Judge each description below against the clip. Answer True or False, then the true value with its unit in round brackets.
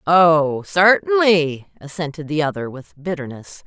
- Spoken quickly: False (115 wpm)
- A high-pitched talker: False (160 Hz)